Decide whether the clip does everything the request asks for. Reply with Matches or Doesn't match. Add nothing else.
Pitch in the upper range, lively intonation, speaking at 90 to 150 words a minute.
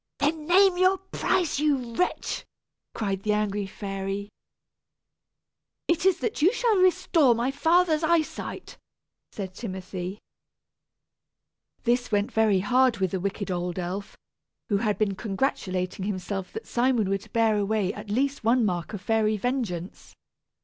Matches